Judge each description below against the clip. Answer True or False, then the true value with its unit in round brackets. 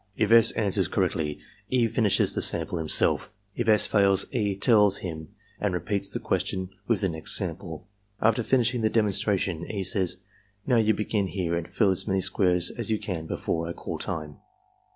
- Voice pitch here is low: True (100 Hz)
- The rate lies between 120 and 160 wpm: False (180 wpm)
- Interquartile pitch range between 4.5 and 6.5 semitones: False (3.6 semitones)